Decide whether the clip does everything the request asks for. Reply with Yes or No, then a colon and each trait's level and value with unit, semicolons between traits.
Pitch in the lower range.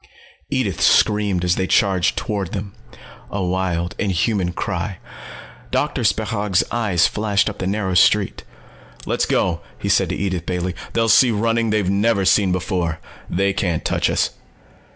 Yes: very low, 95 Hz